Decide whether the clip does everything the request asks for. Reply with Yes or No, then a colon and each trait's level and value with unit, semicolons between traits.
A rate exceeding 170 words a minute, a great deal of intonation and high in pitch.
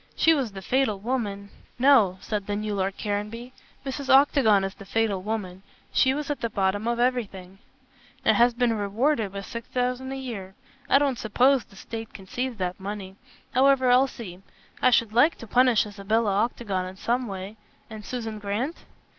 No: average, 185 wpm; average, 4.1 semitones; high, 225 Hz